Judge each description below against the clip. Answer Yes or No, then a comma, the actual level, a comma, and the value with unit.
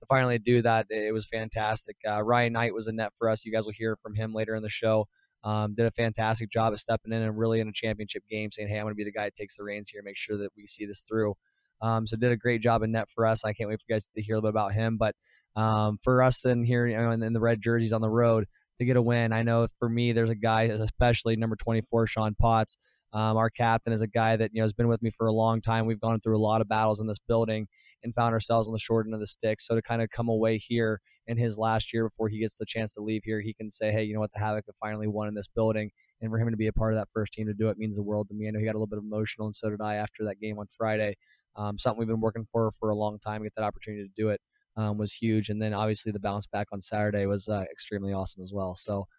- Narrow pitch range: Yes, narrow, 1.1 semitones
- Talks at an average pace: No, fast, 310 wpm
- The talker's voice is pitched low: Yes, low, 110 Hz